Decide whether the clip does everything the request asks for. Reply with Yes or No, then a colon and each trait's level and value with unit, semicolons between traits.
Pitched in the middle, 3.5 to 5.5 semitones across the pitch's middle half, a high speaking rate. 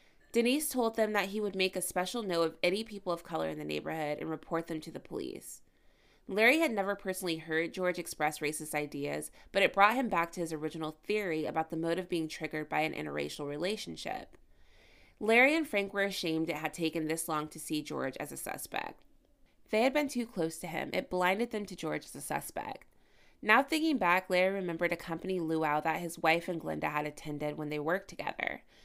Yes: medium, 170 Hz; average, 4.1 semitones; fast, 210 wpm